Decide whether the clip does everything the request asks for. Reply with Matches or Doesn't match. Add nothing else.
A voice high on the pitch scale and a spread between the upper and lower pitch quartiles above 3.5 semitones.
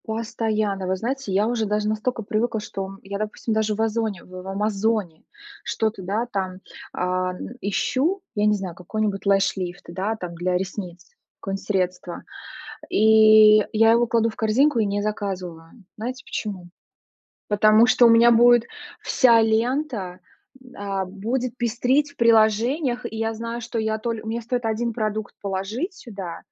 Doesn't match